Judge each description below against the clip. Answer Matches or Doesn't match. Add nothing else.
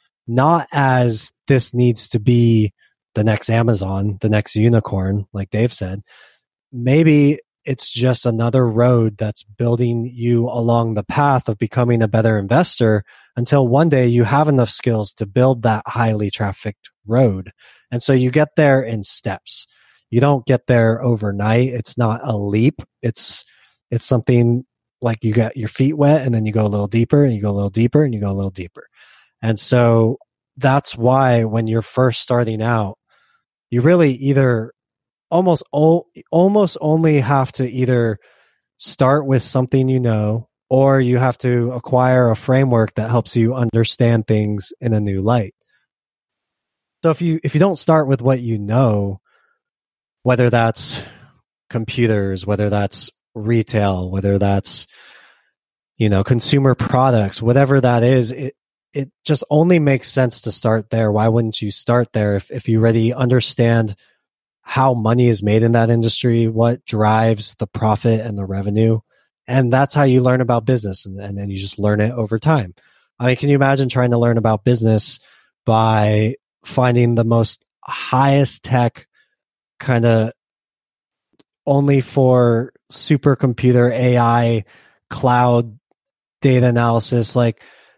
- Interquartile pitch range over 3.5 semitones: Doesn't match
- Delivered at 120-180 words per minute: Matches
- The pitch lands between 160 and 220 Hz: Doesn't match